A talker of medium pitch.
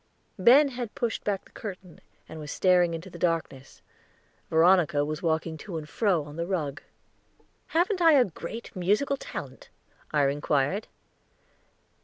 Yes: medium, 175 Hz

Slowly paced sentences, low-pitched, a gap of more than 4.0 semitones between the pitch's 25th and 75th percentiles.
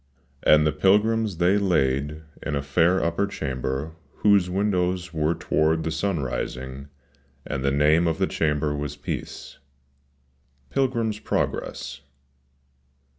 Yes: slow, 125 wpm; very low, 80 Hz; average, 5.1 semitones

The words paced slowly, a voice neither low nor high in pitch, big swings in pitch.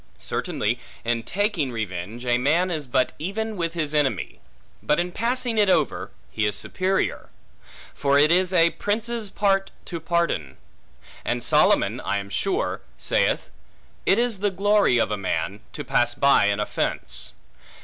No: average, 155 wpm; medium, 165 Hz; wide, 8.7 semitones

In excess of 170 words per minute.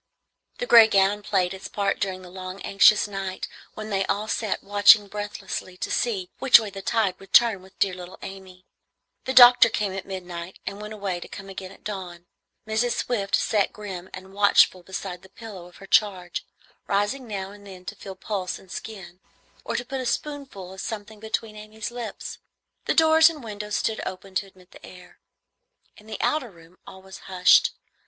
Yes: average, 190 wpm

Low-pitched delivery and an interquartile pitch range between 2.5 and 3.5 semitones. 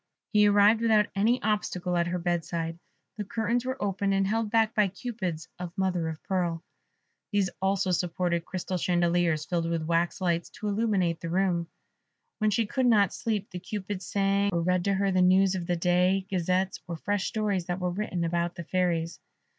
No: medium, 185 Hz; average, 2.9 semitones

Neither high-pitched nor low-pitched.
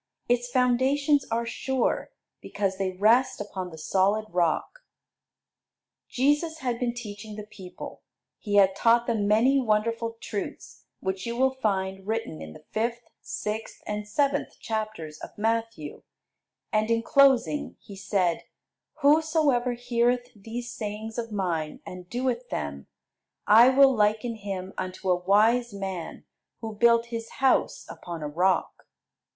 No: high, 220 Hz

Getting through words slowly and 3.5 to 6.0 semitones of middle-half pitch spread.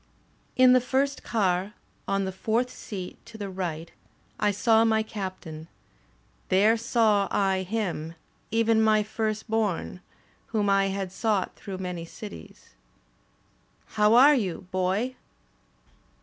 No: slow, 120 wpm; average, 3.1 semitones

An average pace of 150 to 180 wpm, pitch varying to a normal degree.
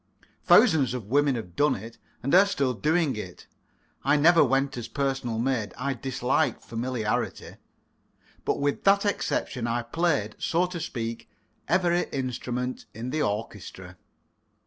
No: average, 140 wpm; average, 4.4 semitones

